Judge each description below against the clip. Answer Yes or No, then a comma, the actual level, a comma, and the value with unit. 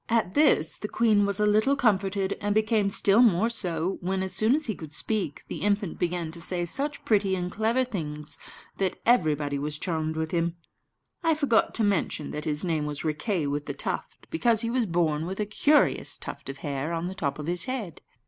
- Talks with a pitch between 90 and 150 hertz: No, high, 190 Hz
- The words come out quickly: Yes, fast, 210 wpm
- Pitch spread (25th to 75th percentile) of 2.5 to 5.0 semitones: No, wide, 5.4 semitones